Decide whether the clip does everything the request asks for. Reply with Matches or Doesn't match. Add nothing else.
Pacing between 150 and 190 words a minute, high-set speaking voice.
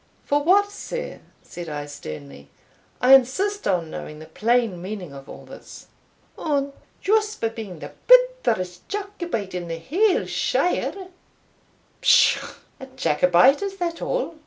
Doesn't match